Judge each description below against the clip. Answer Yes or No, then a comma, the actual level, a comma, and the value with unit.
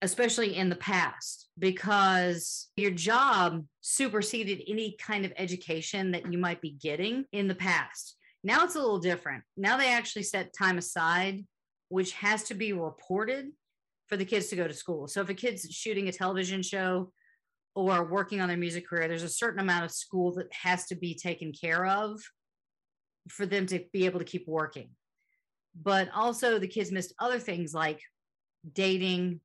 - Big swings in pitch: No, average, 2.8 semitones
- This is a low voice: No, high, 190 Hz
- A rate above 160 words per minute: Yes, average, 175 wpm